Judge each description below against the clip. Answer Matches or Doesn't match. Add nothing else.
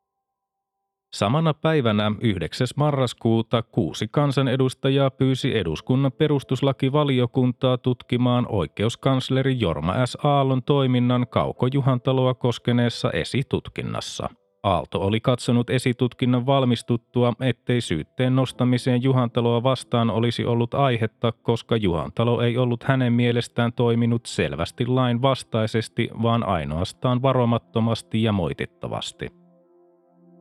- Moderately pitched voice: Doesn't match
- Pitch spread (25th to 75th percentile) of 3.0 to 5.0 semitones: Doesn't match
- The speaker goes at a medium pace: Doesn't match